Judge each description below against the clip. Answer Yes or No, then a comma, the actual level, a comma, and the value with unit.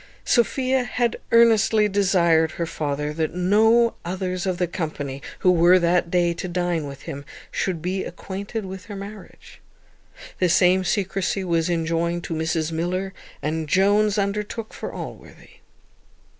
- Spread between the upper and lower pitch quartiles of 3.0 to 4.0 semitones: Yes, average, 3.3 semitones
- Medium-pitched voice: Yes, medium, 180 Hz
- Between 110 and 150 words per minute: Yes, average, 145 wpm